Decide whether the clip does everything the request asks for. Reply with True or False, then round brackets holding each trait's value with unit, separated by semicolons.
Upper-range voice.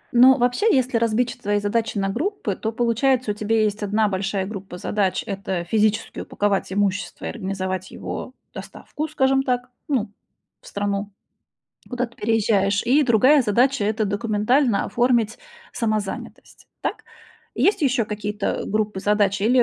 True (215 Hz)